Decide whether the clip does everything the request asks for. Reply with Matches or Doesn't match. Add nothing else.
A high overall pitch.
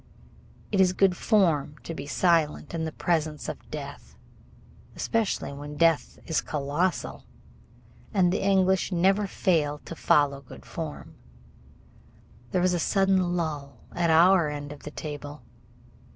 Doesn't match